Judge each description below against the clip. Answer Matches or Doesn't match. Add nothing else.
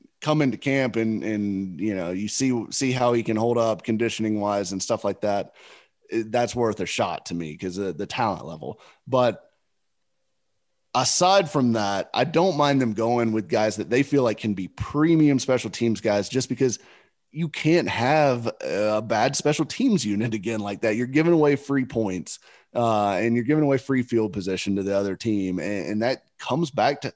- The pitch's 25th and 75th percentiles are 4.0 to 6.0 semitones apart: Matches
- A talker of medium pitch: Doesn't match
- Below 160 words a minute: Doesn't match